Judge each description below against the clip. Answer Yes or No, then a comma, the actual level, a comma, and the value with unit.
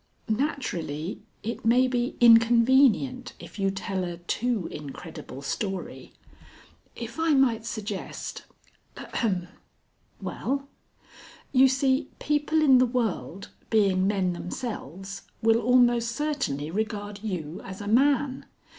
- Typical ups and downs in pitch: Yes, average, 5.0 semitones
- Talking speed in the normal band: No, slow, 115 wpm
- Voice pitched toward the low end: No, high, 225 Hz